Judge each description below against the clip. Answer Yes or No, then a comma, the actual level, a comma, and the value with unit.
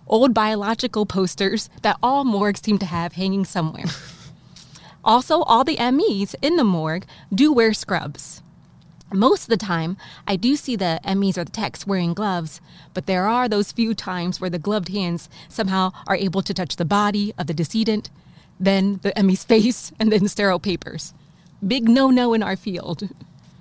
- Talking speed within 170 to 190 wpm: Yes, average, 180 wpm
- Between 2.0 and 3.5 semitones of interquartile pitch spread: No, average, 4.1 semitones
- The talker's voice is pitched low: No, high, 195 Hz